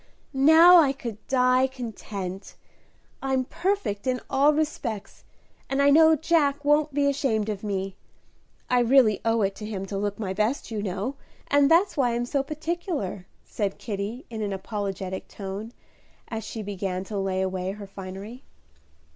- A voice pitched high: Yes, high, 225 Hz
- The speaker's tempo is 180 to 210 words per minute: No, average, 160 wpm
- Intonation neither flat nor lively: No, wide, 6.0 semitones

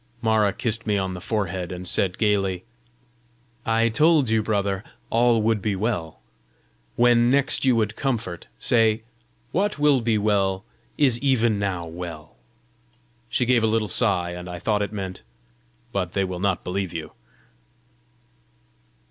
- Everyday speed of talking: Yes, average, 150 wpm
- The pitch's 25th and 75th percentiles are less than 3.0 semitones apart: No, average, 3.7 semitones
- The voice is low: Yes, low, 105 Hz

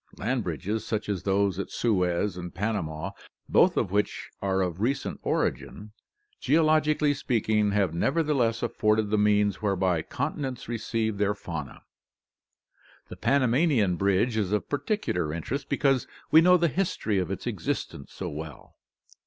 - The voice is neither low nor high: No, low, 105 Hz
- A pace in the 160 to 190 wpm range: No, average, 145 wpm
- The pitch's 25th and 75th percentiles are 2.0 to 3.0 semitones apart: No, wide, 5.6 semitones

